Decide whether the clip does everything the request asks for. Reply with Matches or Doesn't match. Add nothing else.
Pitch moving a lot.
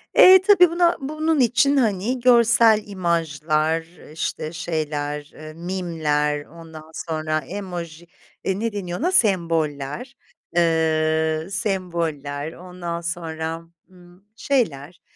Doesn't match